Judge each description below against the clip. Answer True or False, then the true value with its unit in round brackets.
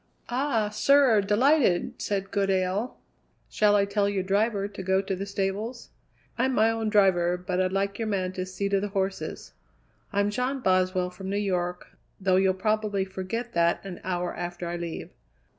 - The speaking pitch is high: True (195 Hz)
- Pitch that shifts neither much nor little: False (2.3 semitones)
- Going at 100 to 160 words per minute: False (175 wpm)